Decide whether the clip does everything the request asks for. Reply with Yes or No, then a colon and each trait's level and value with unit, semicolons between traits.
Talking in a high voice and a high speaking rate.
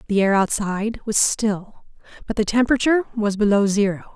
No: high, 210 Hz; average, 160 wpm